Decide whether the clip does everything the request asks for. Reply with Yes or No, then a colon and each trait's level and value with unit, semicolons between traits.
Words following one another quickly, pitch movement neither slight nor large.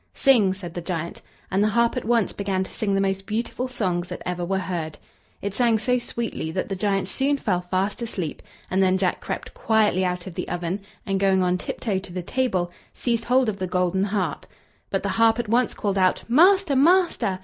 Yes: fast, 215 wpm; average, 4.0 semitones